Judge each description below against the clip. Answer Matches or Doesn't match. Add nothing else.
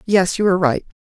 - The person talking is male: Doesn't match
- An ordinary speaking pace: Doesn't match